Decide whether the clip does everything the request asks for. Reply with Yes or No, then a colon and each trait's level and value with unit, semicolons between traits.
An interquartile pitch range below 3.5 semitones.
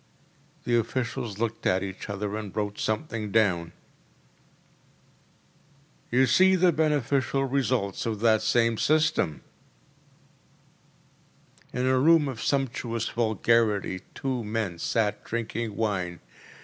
No: average, 3.9 semitones